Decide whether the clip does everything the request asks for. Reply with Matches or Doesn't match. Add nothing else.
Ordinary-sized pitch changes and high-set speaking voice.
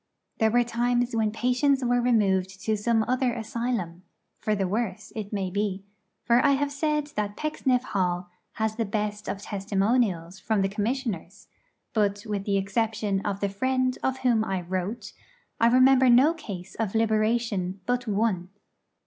Matches